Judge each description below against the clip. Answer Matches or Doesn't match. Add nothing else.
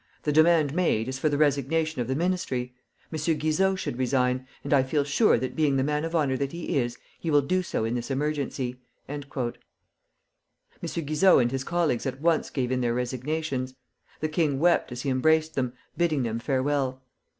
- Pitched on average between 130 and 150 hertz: Matches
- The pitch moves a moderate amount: Matches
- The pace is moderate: Matches